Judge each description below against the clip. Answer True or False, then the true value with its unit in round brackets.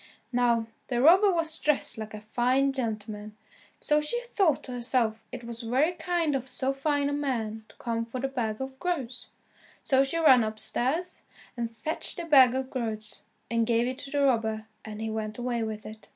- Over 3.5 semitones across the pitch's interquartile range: True (4.1 semitones)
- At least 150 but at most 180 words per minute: False (195 wpm)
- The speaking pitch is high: True (250 Hz)